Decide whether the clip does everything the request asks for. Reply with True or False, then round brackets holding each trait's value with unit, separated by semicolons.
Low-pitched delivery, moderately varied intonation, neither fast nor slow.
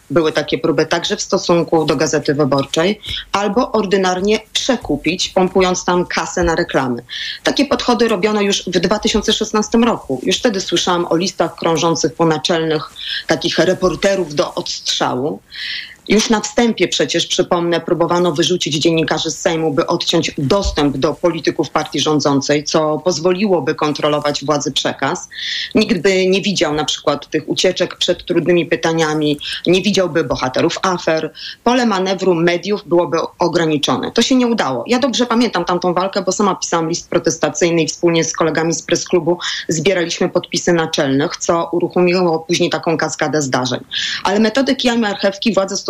False (175 Hz; 3.4 semitones; 150 wpm)